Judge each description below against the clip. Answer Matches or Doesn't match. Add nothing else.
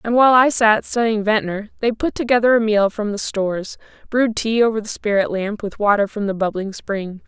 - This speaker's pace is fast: Matches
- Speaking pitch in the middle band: Doesn't match